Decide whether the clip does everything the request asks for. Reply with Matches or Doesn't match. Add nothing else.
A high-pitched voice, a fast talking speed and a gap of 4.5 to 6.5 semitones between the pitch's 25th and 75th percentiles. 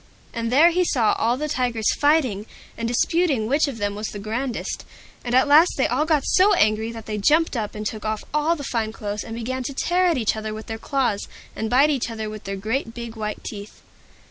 Matches